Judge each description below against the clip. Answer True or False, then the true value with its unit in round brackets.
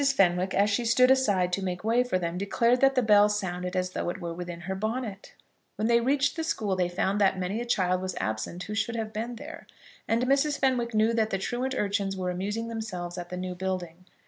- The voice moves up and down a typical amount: True (4.3 semitones)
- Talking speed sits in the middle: False (230 wpm)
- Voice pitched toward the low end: False (200 Hz)